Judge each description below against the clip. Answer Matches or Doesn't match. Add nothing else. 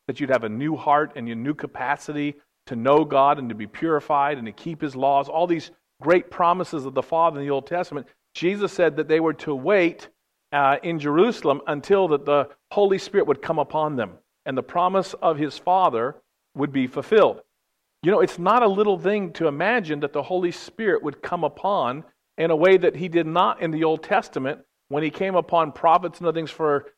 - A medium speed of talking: Doesn't match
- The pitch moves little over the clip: Doesn't match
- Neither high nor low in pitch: Matches